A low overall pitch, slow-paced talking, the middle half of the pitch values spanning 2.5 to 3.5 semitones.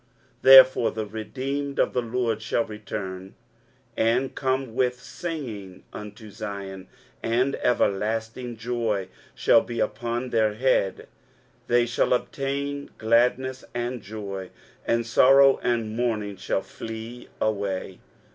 Yes: low, 115 Hz; slow, 120 wpm; average, 3.2 semitones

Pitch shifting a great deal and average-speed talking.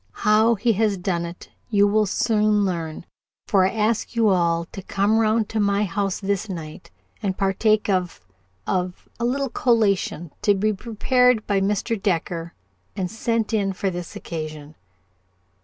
No: average, 3.1 semitones; average, 155 wpm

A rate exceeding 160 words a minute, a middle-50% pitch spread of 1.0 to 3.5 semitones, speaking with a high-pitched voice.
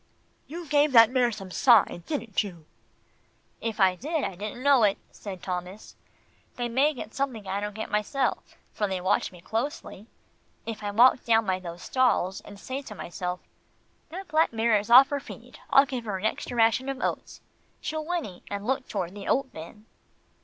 No: average, 190 wpm; average, 5.2 semitones; high, 225 Hz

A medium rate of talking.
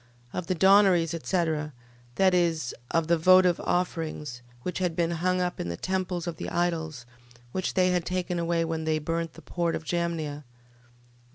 Yes: average, 180 wpm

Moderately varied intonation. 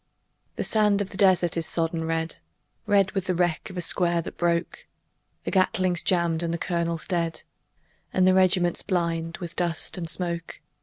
No: narrow, 1.9 semitones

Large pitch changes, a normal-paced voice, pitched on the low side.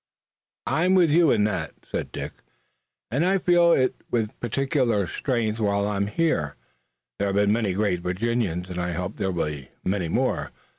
Yes: wide, 6.5 semitones; average, 175 wpm; low, 105 Hz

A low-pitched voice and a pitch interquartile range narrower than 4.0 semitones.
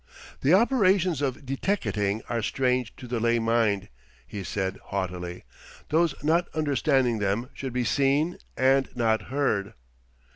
No: low, 125 Hz; average, 5.2 semitones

